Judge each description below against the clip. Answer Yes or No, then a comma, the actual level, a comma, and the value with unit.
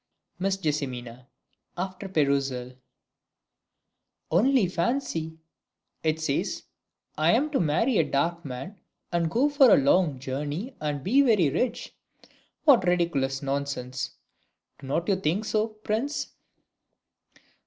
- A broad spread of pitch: Yes, wide, 7.2 semitones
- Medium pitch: Yes, medium, 170 Hz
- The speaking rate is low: Yes, slow, 110 wpm